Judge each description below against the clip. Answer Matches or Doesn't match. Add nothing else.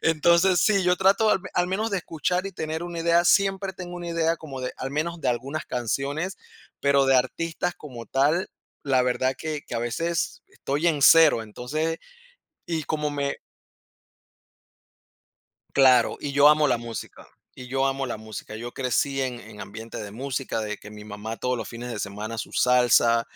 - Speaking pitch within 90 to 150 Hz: Matches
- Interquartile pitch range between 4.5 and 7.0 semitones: Matches